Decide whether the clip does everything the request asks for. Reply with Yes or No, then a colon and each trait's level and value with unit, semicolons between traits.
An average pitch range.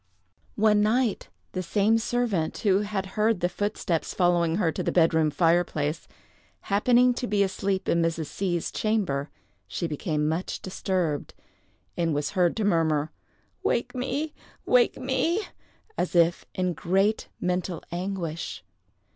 Yes: average, 4.2 semitones